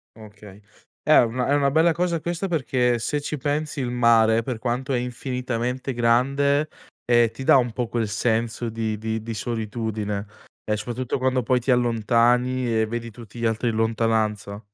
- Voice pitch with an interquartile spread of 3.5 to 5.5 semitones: No, narrow, 2.4 semitones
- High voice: No, low, 120 Hz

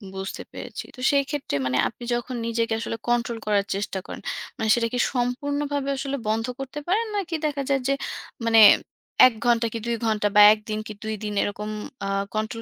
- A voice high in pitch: Yes, high, 235 Hz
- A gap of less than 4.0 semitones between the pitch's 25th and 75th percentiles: No, average, 4.3 semitones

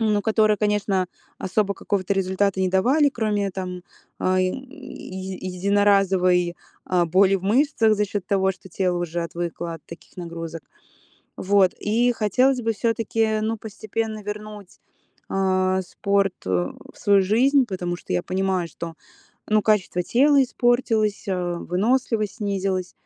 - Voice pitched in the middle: No, high, 200 Hz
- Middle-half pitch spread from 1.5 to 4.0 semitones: Yes, average, 2.8 semitones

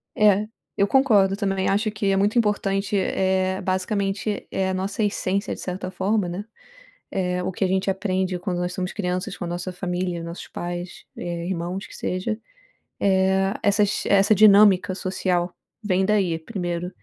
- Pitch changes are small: Yes, narrow, 1.8 semitones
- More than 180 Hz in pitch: Yes, high, 190 Hz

